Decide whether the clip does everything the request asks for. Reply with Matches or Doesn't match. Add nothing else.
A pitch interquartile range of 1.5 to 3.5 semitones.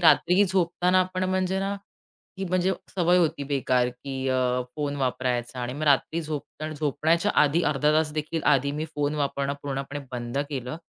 Doesn't match